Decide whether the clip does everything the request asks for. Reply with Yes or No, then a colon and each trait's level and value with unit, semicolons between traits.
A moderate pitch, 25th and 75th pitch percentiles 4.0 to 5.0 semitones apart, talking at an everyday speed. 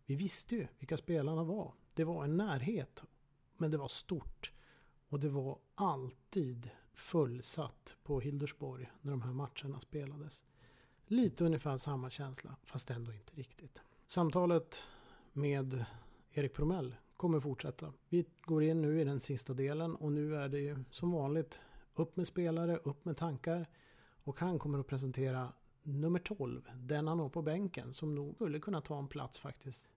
No: medium, 145 Hz; average, 3.5 semitones; average, 160 wpm